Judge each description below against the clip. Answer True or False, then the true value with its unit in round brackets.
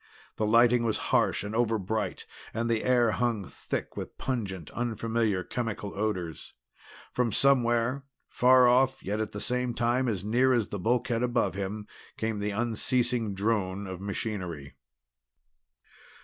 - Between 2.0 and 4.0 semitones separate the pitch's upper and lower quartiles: True (3.0 semitones)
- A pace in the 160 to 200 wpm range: False (140 wpm)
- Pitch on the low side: True (115 Hz)